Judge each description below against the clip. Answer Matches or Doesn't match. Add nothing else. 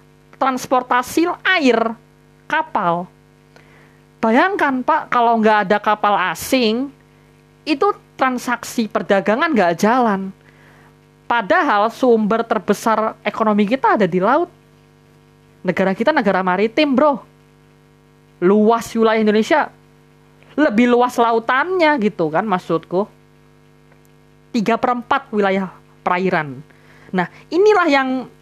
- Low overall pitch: Doesn't match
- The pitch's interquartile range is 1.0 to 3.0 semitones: Doesn't match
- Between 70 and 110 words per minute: Matches